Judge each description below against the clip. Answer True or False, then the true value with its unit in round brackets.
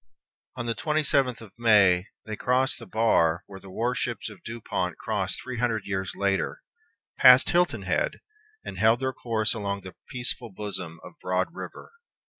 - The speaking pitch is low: True (110 Hz)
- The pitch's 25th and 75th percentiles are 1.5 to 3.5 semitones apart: False (4.3 semitones)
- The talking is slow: False (170 wpm)